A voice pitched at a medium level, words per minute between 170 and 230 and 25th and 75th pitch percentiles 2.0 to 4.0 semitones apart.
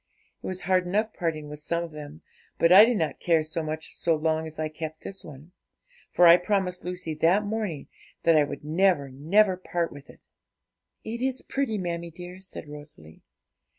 Yes: medium, 170 Hz; average, 190 wpm; average, 3.3 semitones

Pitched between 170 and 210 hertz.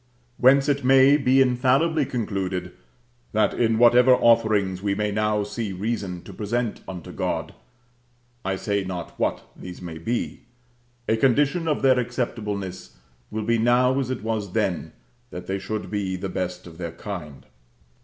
No: low, 110 Hz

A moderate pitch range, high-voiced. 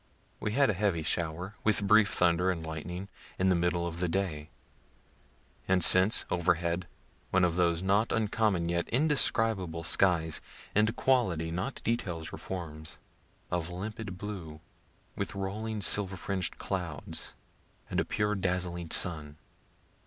No: average, 3.3 semitones; very low, 90 Hz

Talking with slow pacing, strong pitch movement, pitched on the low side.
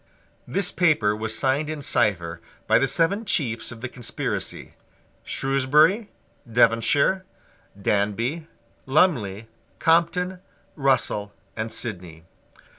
Yes: slow, 100 wpm; wide, 6.9 semitones; low, 130 Hz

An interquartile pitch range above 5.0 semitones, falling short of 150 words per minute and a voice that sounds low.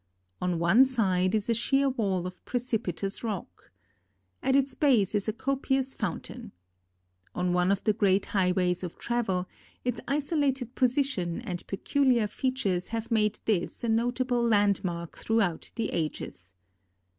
No: wide, 5.6 semitones; average, 140 wpm; high, 215 Hz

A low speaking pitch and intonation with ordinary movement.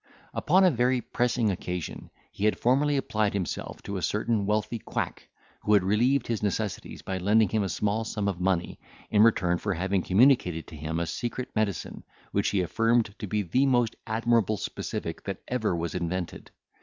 Yes: low, 105 Hz; average, 3.9 semitones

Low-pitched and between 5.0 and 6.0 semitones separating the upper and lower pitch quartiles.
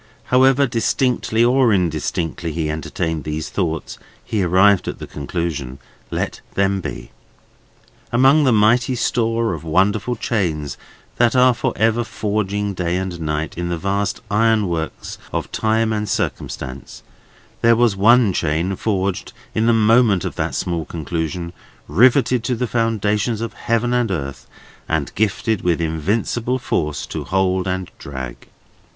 Yes: low, 100 Hz; wide, 5.5 semitones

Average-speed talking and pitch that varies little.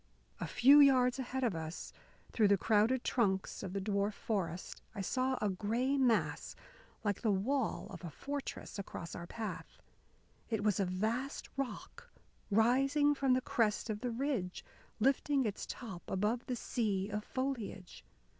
No: average, 155 wpm; average, 4.7 semitones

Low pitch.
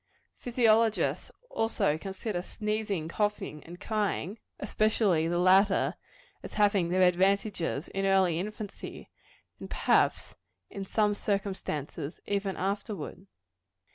No: high, 195 Hz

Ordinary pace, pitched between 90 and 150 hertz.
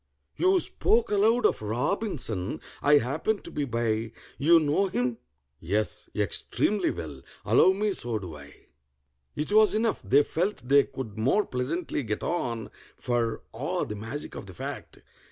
Yes: average, 150 wpm; low, 135 Hz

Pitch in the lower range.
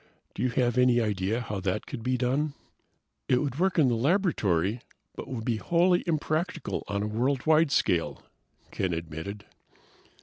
Yes: low, 125 Hz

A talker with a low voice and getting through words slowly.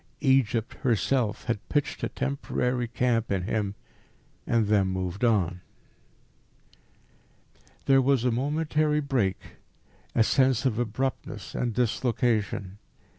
Yes: low, 120 Hz; slow, 110 wpm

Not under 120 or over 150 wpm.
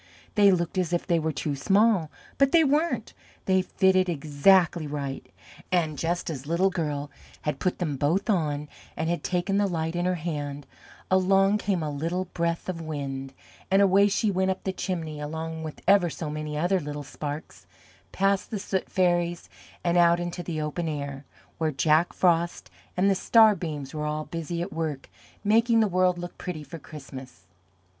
No: average, 180 wpm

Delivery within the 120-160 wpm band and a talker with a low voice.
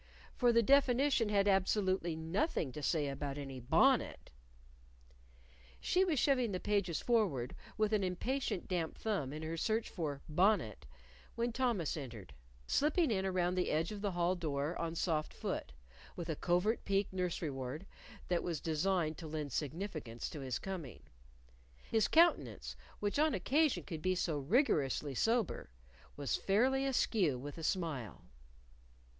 No: average, 150 wpm; medium, 180 Hz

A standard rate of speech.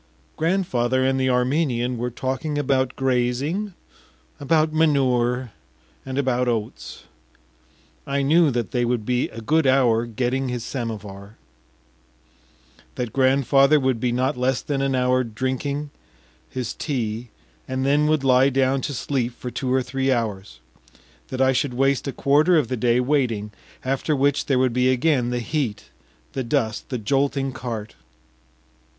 Yes: average, 150 wpm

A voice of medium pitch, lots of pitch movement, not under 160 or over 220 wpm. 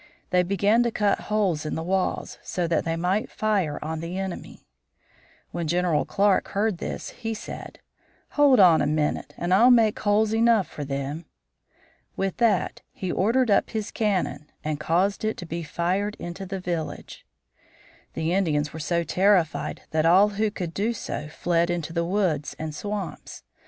No: medium, 180 Hz; average, 4.1 semitones; average, 170 wpm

